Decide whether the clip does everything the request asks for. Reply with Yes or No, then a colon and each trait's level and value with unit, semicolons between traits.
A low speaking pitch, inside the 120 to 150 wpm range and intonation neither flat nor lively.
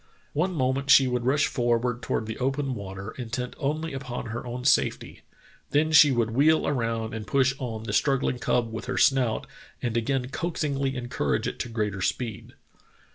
No: low, 125 Hz; average, 175 wpm; average, 3.3 semitones